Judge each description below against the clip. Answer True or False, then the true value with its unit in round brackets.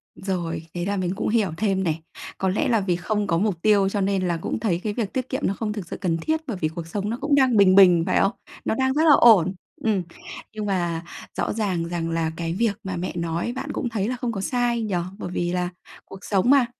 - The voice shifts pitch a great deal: False (4.2 semitones)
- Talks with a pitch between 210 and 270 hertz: False (195 Hz)